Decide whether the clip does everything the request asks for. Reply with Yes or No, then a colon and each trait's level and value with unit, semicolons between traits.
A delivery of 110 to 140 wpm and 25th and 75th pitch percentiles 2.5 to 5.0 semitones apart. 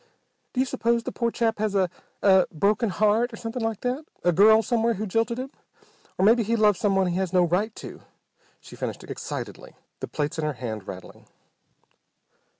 No: average, 190 wpm; average, 4.0 semitones